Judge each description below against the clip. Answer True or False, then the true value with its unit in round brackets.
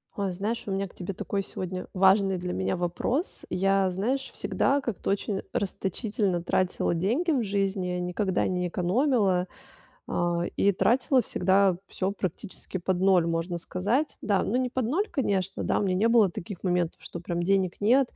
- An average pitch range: True (3.1 semitones)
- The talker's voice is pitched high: True (195 Hz)